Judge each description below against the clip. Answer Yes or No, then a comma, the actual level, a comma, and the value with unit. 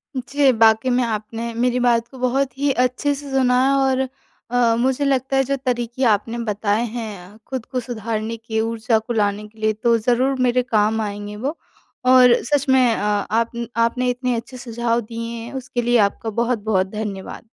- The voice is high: Yes, high, 235 Hz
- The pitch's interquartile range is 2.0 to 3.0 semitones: Yes, narrow, 2.5 semitones